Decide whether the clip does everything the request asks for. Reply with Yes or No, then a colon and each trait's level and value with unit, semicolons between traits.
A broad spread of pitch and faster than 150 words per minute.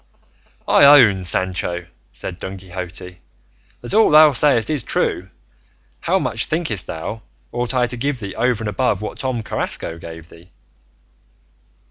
No: wide, 6.0 semitones; average, 145 wpm